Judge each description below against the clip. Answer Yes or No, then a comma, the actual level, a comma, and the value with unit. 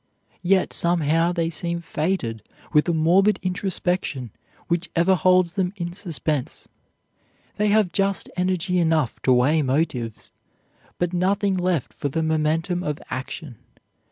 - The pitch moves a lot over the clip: No, average, 3.1 semitones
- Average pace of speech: No, slow, 130 wpm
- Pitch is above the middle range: No, medium, 170 Hz